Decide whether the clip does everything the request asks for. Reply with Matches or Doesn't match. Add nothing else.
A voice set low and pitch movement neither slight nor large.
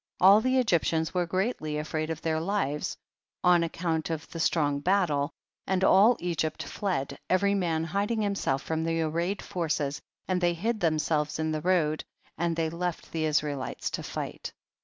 Doesn't match